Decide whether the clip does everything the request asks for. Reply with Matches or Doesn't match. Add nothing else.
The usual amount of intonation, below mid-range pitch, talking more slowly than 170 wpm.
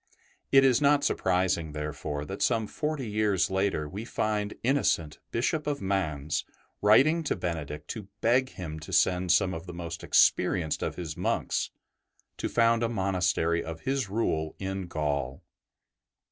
Doesn't match